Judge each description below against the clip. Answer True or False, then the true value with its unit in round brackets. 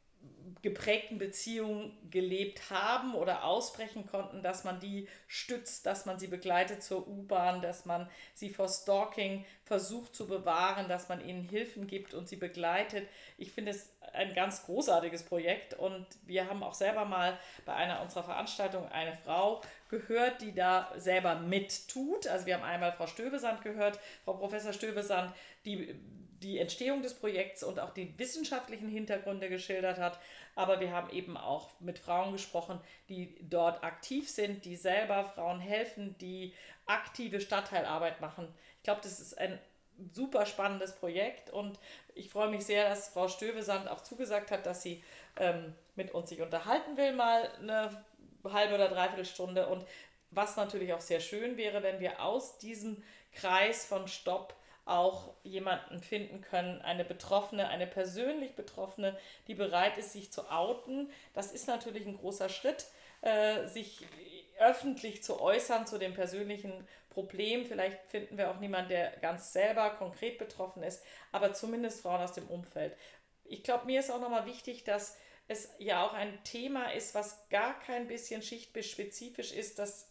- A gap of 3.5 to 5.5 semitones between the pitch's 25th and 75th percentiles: False (2.9 semitones)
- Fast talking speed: False (160 wpm)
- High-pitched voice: True (200 Hz)